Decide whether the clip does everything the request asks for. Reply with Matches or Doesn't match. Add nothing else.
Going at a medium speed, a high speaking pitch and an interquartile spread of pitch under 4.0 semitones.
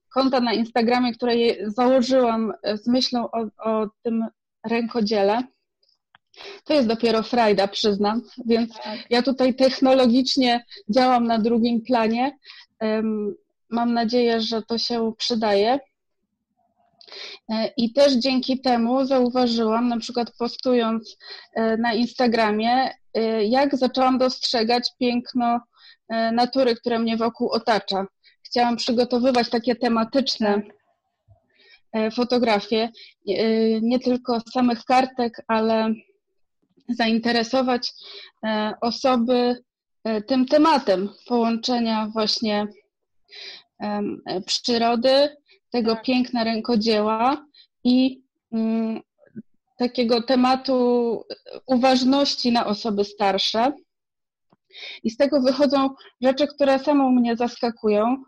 Doesn't match